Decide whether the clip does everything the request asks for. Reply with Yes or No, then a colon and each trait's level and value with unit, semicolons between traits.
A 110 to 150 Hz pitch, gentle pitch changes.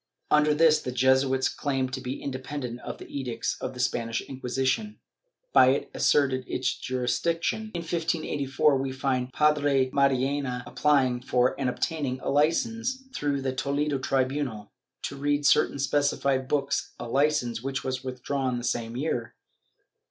Yes: low, 135 Hz; narrow, 2.2 semitones